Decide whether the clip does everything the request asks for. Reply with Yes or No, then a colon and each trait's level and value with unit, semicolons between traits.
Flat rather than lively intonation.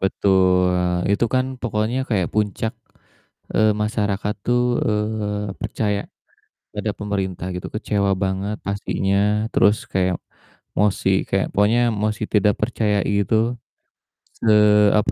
Yes: narrow, 1.9 semitones